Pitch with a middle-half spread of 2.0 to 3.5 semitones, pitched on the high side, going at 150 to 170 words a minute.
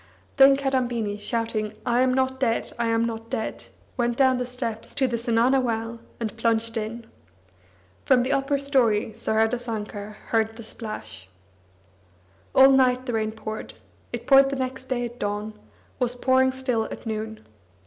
Yes: average, 2.7 semitones; high, 235 Hz; average, 155 wpm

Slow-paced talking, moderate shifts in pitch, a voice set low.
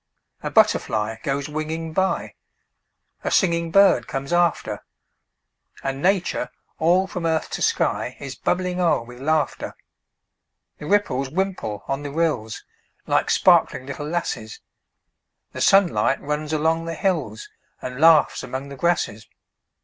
No: slow, 130 wpm; average, 4.4 semitones; medium, 155 Hz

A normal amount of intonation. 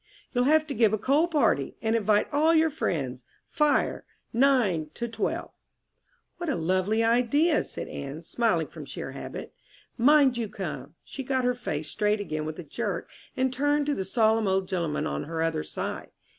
No: wide, 8.6 semitones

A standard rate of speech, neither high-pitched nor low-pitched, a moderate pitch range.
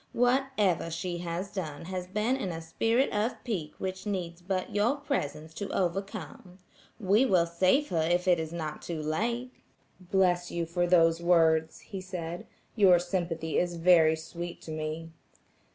Yes: average, 160 wpm; medium, 175 Hz; average, 3.1 semitones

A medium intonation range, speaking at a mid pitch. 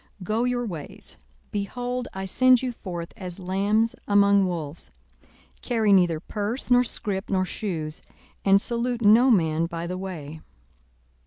No: average, 4.7 semitones; high, 200 Hz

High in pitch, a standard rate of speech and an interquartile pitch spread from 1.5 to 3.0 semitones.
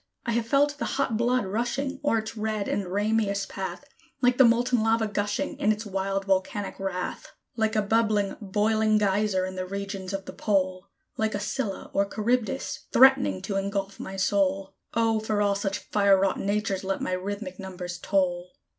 Yes: high, 205 Hz; average, 180 wpm; narrow, 2.5 semitones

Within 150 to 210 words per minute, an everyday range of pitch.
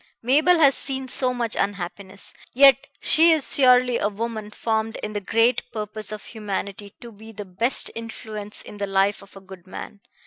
Yes: average, 180 wpm; average, 3.6 semitones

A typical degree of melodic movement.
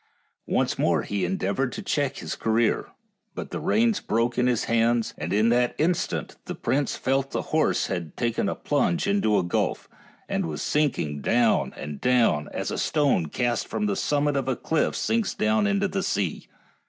No: wide, 6.1 semitones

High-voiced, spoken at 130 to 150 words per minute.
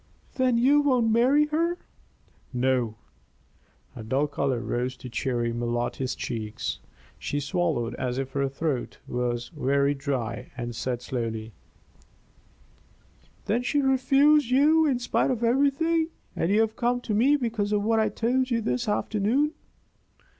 Yes: high, 205 Hz; average, 140 wpm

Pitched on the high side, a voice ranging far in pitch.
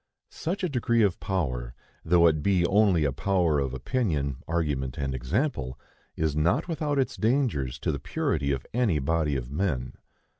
No: very low, 80 Hz; wide, 7.2 semitones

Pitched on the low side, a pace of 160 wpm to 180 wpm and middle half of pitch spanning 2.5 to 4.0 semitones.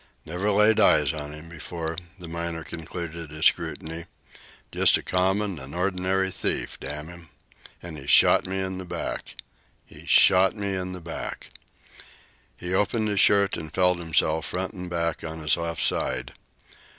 Yes: very low, 85 Hz; average, 165 wpm; average, 2.8 semitones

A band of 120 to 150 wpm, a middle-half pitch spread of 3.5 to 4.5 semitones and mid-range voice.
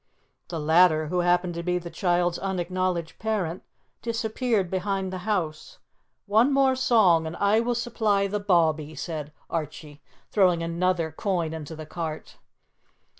Yes: average, 140 wpm; average, 3.8 semitones; medium, 180 Hz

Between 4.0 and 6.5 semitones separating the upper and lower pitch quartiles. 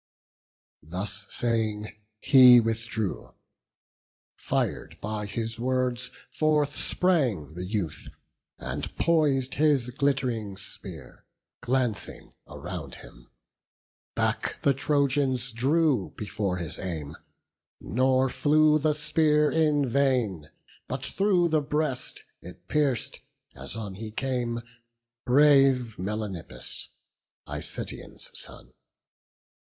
Yes: average, 5.3 semitones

